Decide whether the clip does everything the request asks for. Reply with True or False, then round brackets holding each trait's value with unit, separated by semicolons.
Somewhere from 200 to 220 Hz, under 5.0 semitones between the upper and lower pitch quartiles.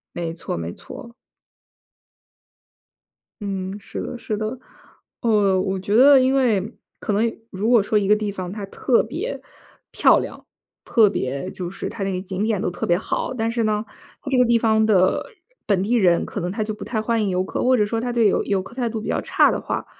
True (210 Hz; 3.4 semitones)